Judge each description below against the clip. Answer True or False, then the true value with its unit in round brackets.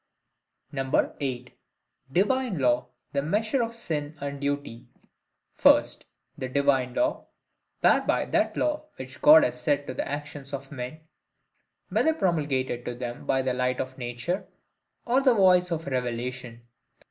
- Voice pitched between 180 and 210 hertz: False (140 Hz)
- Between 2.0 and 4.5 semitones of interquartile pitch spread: False (5.0 semitones)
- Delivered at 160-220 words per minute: False (135 wpm)